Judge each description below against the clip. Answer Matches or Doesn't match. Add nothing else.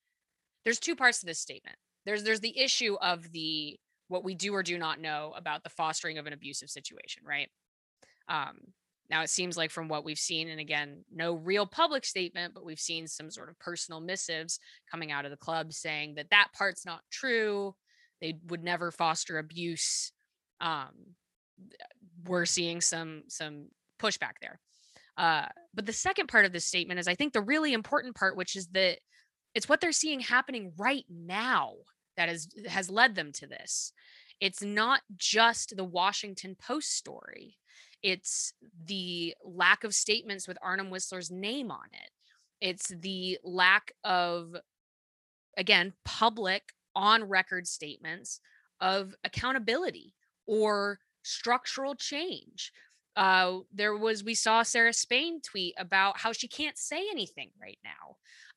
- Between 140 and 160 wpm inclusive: Matches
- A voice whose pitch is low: Doesn't match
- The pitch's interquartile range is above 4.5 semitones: Matches